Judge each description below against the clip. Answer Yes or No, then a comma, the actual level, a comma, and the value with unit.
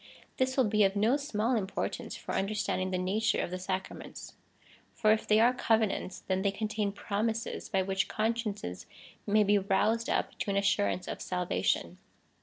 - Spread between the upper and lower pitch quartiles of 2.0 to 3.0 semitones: Yes, narrow, 2.5 semitones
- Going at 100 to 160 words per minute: No, average, 175 wpm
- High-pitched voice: Yes, high, 210 Hz